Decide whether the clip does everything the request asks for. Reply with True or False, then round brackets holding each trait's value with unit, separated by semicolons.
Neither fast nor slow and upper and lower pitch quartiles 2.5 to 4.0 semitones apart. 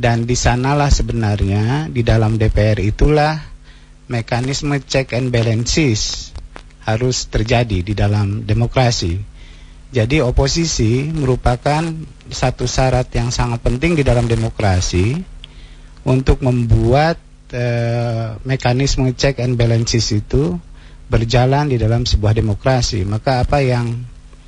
True (110 wpm; 3.1 semitones)